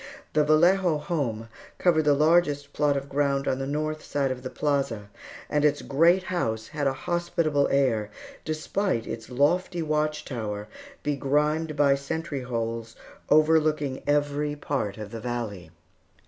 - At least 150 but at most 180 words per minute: No, average, 140 wpm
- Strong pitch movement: No, average, 3.3 semitones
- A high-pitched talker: No, medium, 145 Hz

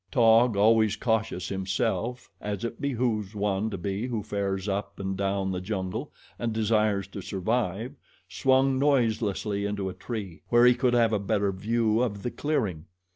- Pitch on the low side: Yes, low, 105 Hz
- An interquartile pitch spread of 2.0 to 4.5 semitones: Yes, average, 3.2 semitones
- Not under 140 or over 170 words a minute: Yes, average, 165 wpm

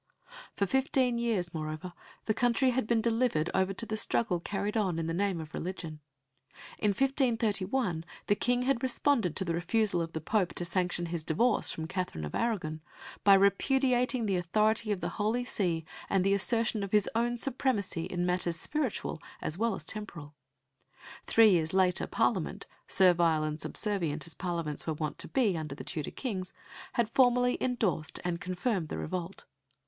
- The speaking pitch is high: Yes, high, 195 Hz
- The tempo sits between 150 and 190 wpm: Yes, average, 175 wpm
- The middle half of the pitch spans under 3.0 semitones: No, wide, 5.4 semitones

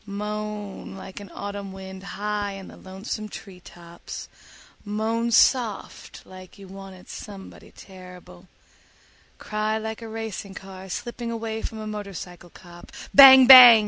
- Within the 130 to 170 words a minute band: Yes, slow, 135 wpm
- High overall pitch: Yes, high, 205 Hz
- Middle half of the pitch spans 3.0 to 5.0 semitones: No, narrow, 2.6 semitones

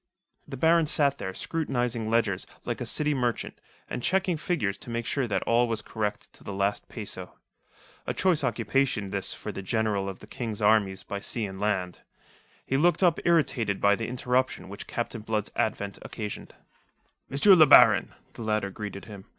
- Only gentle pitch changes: No, average, 4.8 semitones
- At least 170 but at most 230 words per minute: Yes, average, 180 wpm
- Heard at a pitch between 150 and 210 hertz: No, low, 115 Hz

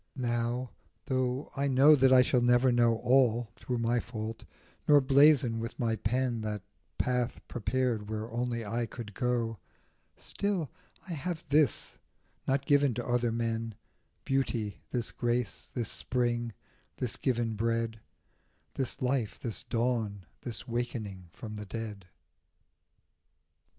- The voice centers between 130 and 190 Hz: No, low, 120 Hz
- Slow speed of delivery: Yes, slow, 130 wpm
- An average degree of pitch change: No, narrow, 2.3 semitones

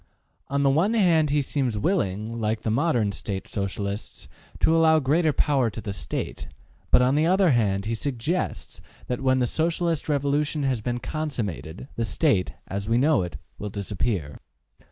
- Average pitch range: No, wide, 6.5 semitones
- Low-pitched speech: Yes, low, 125 Hz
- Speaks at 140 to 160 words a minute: No, average, 170 wpm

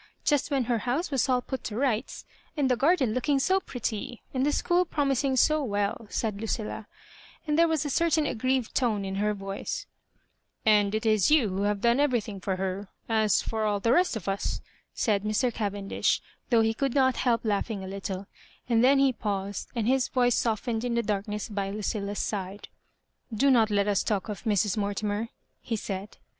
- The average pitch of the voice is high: Yes, high, 225 Hz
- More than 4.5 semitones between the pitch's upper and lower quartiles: No, average, 4.2 semitones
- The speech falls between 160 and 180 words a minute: No, average, 200 wpm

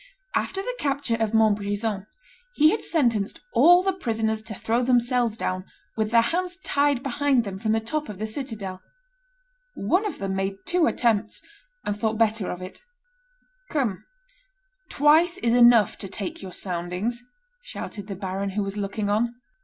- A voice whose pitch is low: No, high, 225 Hz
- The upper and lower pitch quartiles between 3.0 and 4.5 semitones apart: No, average, 5.2 semitones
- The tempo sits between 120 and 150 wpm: No, average, 160 wpm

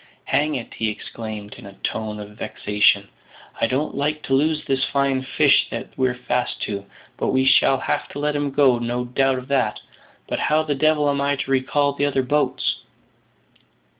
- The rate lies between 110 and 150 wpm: No, average, 190 wpm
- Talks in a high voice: No, low, 135 Hz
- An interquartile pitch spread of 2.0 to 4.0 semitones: Yes, average, 3.3 semitones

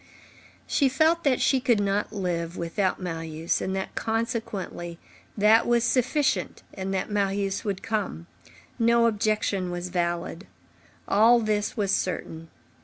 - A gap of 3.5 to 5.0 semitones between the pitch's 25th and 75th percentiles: Yes, average, 4.0 semitones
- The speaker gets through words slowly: Yes, slow, 130 wpm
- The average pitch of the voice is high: Yes, high, 200 Hz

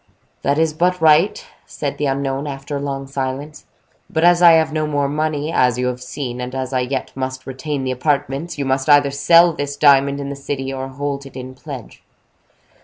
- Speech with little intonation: Yes, narrow, 2.3 semitones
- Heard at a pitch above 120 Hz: Yes, medium, 140 Hz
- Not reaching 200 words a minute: No, fast, 205 wpm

